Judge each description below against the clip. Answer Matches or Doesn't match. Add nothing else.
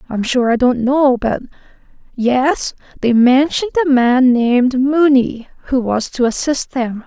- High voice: Matches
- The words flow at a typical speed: Matches